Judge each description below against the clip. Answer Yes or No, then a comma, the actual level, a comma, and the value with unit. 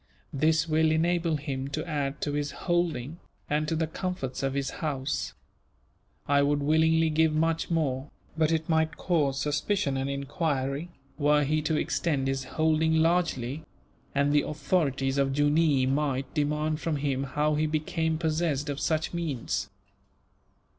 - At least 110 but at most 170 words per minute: Yes, average, 150 wpm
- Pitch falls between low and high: Yes, medium, 150 Hz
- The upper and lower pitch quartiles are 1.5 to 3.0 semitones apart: Yes, narrow, 2.5 semitones